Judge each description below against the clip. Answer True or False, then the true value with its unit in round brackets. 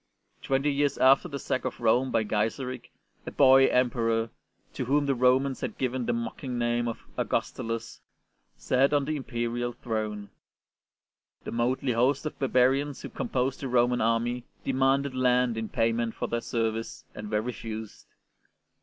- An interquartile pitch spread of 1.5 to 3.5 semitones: True (2.5 semitones)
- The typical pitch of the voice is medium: False (125 Hz)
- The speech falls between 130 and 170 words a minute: True (155 wpm)